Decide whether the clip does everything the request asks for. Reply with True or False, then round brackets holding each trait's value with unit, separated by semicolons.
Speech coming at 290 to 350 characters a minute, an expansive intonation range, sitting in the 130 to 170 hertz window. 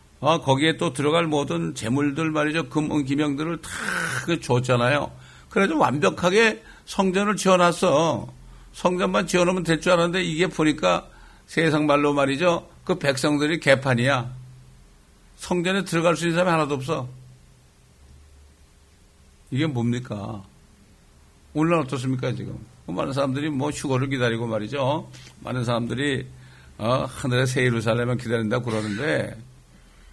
True (295 characters per minute; 7.1 semitones; 135 Hz)